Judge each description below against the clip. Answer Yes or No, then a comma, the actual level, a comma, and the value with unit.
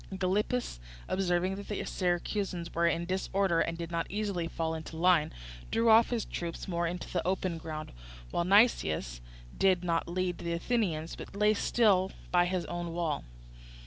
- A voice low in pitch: No, medium, 175 Hz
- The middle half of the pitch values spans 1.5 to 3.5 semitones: Yes, narrow, 2.6 semitones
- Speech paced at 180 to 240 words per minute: No, average, 170 wpm